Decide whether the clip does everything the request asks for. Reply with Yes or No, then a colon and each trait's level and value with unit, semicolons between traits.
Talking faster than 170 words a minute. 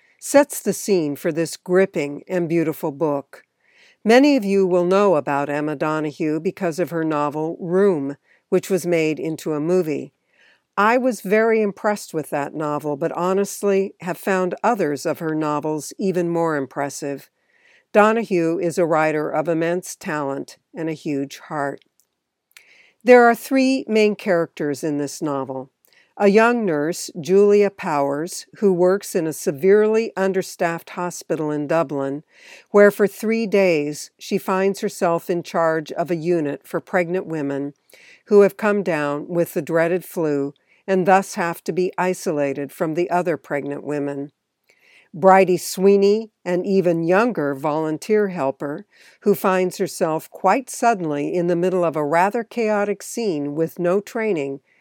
No: average, 150 wpm